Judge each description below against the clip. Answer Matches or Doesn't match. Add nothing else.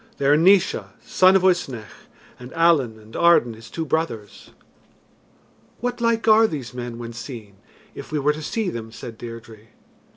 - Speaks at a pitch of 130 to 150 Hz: Matches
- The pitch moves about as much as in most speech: Doesn't match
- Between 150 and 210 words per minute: Matches